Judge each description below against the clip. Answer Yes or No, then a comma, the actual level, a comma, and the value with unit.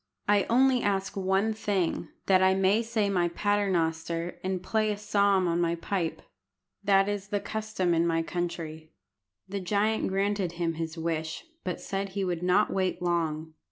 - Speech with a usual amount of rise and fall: Yes, average, 3.1 semitones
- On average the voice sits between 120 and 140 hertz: No, high, 190 Hz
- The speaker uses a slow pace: No, average, 165 wpm